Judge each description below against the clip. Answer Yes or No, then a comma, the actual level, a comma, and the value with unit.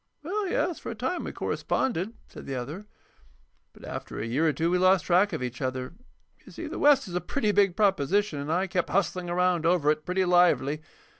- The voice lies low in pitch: No, medium, 180 Hz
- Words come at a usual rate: No, fast, 215 wpm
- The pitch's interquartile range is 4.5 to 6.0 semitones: Yes, average, 4.8 semitones